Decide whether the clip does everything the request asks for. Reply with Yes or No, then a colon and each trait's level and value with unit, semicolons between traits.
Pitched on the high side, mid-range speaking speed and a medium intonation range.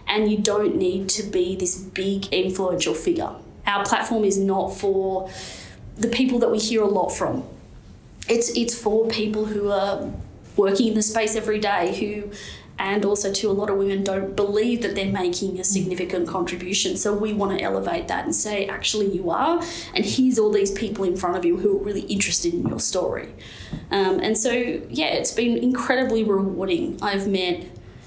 No: high, 200 Hz; average, 190 wpm; narrow, 2.3 semitones